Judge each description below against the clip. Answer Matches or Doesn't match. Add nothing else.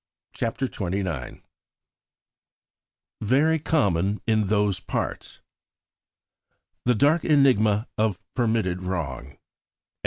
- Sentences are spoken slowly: Matches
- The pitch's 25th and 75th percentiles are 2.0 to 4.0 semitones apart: Doesn't match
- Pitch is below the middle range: Matches